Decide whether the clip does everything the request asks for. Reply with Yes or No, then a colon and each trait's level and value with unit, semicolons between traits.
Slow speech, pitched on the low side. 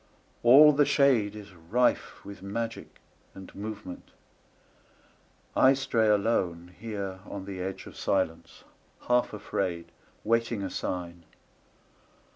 Yes: slow, 95 wpm; low, 100 Hz